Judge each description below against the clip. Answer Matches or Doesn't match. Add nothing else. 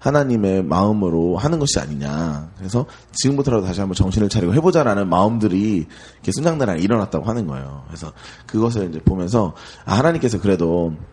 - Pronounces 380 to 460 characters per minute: Matches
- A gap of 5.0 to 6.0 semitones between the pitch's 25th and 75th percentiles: Matches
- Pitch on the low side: Matches